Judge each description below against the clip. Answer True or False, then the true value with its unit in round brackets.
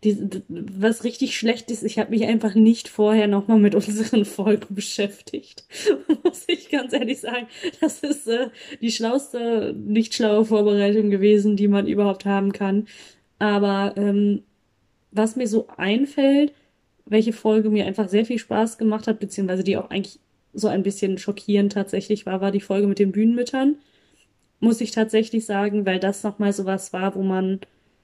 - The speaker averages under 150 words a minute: False (165 wpm)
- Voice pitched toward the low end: False (215 Hz)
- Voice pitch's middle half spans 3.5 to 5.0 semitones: False (2.4 semitones)